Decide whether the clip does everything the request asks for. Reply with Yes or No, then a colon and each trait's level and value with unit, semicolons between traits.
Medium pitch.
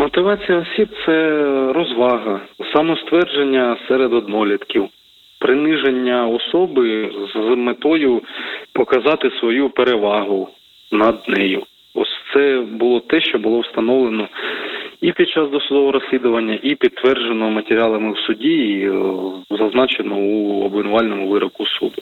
No: low, 125 Hz